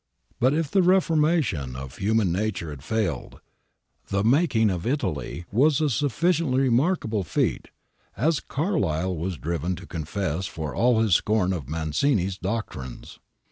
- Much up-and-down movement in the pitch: Yes, wide, 9.0 semitones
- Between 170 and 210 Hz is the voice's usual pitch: No, low, 105 Hz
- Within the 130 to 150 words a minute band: Yes, average, 140 wpm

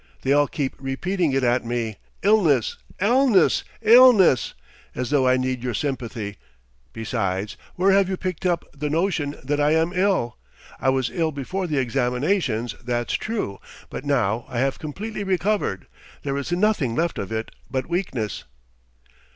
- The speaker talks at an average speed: Yes, average, 155 wpm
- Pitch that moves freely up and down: Yes, wide, 7.1 semitones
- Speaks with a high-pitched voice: No, medium, 140 Hz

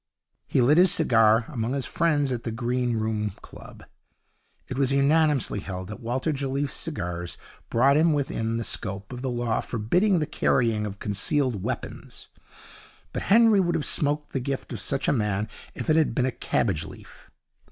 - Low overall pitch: Yes, low, 125 Hz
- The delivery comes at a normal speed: Yes, average, 175 wpm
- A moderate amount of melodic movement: Yes, average, 4.9 semitones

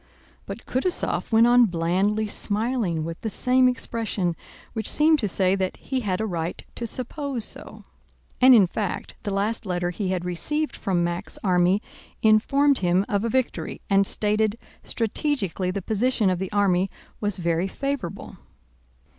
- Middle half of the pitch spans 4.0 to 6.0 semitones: Yes, average, 4.6 semitones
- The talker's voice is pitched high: Yes, high, 205 Hz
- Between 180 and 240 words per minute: No, average, 155 wpm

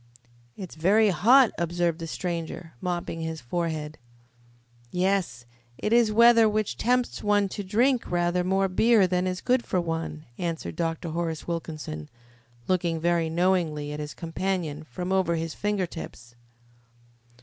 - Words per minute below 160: Yes, average, 140 wpm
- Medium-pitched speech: Yes, medium, 175 Hz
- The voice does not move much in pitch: No, average, 3.2 semitones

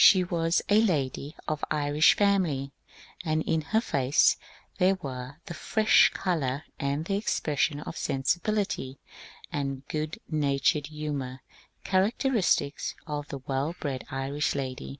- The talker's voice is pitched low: No, medium, 150 Hz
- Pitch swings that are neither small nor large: Yes, average, 4.3 semitones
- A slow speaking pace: Yes, slow, 130 wpm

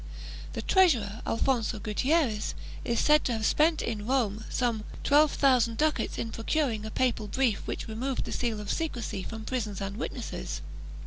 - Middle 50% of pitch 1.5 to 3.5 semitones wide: No, average, 3.9 semitones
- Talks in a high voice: Yes, high, 230 Hz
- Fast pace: No, average, 165 wpm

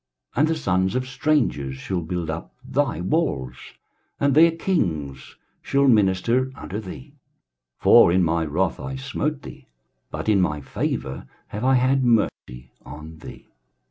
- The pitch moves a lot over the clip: Yes, wide, 9.0 semitones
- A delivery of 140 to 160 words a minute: Yes, average, 150 wpm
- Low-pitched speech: Yes, low, 100 Hz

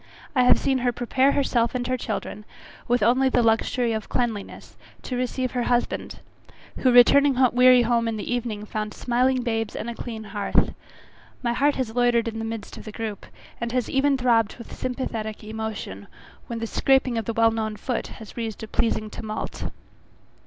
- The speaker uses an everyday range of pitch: No, narrow, 2.2 semitones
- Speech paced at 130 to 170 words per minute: No, average, 180 wpm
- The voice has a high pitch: Yes, high, 235 Hz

